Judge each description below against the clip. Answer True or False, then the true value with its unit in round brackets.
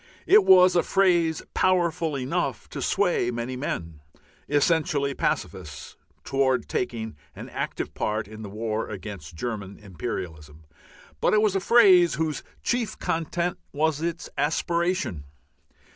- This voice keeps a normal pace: False (130 wpm)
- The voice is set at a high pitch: False (140 Hz)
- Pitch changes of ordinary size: False (8.3 semitones)